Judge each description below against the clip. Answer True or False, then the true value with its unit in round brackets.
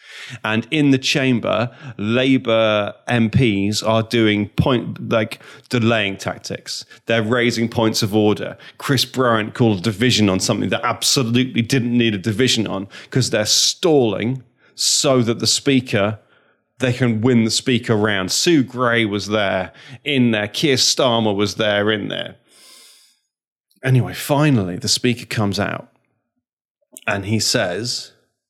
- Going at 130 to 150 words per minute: True (135 wpm)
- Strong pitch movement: False (3.0 semitones)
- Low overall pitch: True (115 Hz)